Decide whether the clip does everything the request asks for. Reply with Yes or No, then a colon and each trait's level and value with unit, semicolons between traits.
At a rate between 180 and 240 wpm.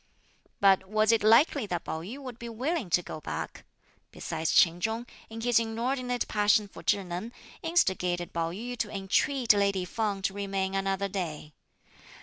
No: average, 165 wpm